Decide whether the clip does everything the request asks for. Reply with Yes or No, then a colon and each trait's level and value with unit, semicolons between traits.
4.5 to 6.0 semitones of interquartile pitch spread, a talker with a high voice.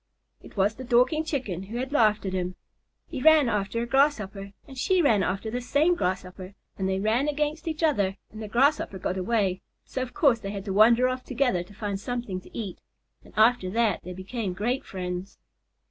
Yes: average, 5.1 semitones; high, 220 Hz